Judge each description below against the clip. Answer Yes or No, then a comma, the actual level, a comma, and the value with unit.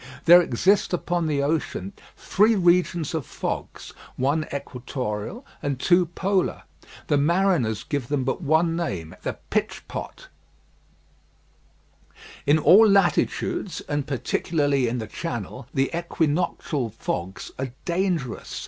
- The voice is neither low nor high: Yes, medium, 155 Hz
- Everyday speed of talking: No, slow, 120 wpm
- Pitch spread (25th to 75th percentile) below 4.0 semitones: No, average, 4.9 semitones